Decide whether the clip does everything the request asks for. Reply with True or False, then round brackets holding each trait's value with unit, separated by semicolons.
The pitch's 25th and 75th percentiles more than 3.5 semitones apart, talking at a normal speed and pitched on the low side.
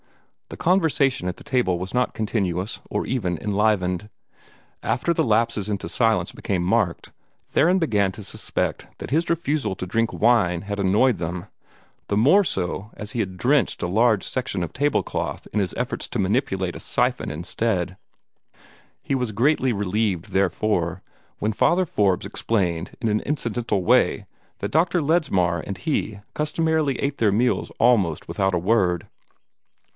True (5.5 semitones; 155 wpm; 105 Hz)